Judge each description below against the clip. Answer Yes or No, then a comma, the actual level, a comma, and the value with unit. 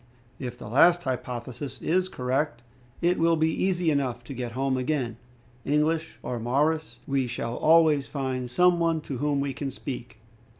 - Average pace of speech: Yes, average, 165 wpm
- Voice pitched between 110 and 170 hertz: Yes, medium, 140 Hz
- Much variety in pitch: No, average, 4.3 semitones